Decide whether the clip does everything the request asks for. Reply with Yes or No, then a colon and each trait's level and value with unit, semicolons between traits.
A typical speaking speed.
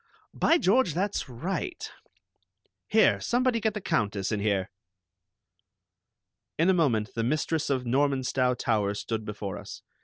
No: slow, 130 wpm